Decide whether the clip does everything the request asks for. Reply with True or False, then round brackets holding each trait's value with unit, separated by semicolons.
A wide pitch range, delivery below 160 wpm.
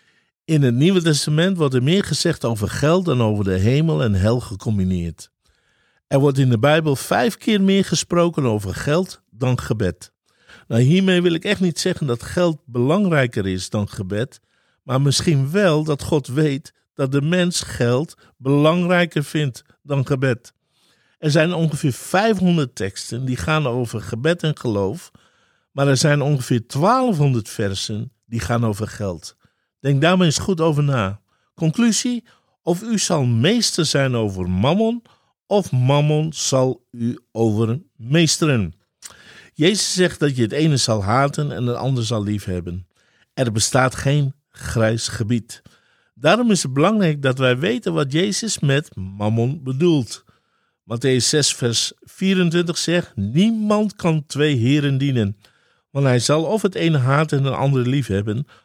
True (6.0 semitones; 150 wpm)